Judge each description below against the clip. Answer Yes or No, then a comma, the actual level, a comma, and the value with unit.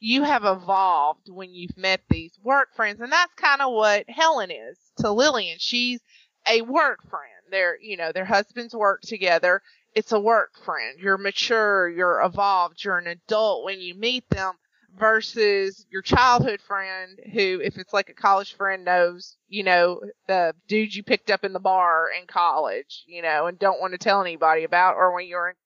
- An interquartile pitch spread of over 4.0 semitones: No, average, 3.6 semitones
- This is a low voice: No, high, 195 Hz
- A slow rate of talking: No, average, 190 wpm